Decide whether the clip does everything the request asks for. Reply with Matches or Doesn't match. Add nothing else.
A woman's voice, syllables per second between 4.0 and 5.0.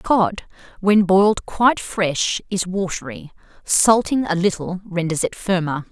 Matches